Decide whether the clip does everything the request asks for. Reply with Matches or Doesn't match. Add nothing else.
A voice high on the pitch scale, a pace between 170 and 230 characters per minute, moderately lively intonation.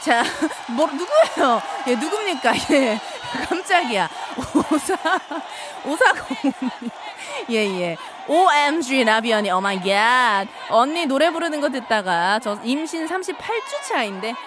Doesn't match